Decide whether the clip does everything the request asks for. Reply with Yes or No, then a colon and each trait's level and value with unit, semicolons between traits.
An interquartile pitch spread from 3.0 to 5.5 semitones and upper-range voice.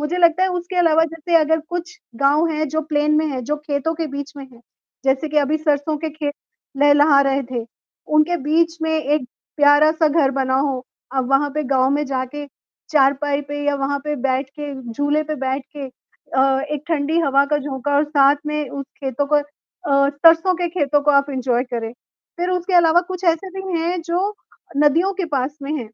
No: narrow, 2.6 semitones; very high, 295 Hz